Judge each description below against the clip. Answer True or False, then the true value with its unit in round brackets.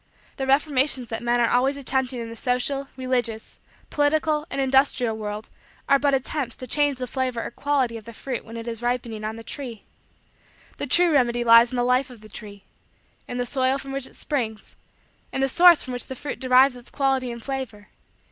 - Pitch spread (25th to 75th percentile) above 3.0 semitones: False (2.7 semitones)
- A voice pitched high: True (255 Hz)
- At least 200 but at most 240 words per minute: True (205 wpm)